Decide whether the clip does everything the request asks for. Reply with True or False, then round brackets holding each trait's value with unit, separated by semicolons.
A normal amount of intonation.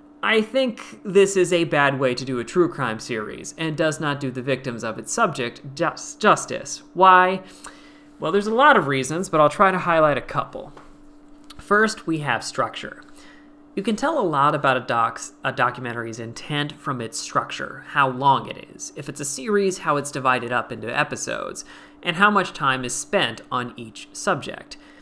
False (7.9 semitones)